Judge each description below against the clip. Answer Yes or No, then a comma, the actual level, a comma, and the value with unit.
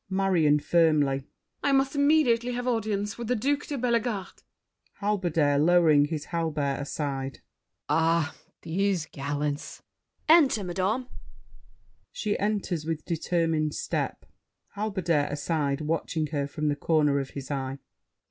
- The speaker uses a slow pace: Yes, slow, 125 wpm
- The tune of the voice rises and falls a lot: Yes, wide, 6.2 semitones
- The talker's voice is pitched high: No, medium, 165 Hz